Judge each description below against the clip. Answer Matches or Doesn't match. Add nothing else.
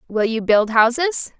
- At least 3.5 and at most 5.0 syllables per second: Matches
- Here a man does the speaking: Doesn't match